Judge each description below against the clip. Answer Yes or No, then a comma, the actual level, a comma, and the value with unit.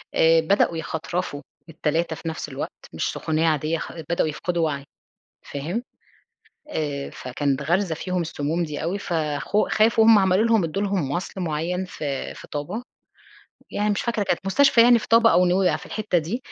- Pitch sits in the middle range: Yes, medium, 170 Hz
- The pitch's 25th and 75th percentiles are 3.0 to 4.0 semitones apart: No, average, 4.6 semitones